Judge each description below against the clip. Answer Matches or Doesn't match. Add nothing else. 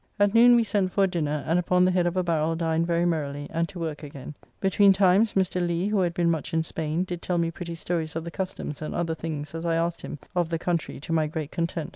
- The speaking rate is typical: Doesn't match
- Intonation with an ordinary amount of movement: Doesn't match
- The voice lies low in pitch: Doesn't match